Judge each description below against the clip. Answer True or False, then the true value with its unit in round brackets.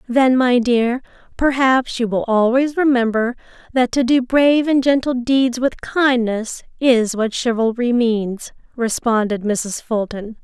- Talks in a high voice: True (245 Hz)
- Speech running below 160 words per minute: True (140 wpm)